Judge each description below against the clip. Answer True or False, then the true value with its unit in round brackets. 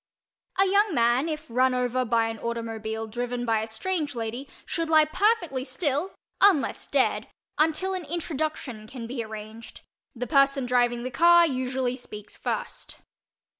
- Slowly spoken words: False (150 wpm)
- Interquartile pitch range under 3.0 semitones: False (5.2 semitones)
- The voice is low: False (255 Hz)